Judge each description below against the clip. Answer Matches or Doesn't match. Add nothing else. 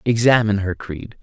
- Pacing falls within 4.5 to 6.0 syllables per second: Matches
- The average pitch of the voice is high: Doesn't match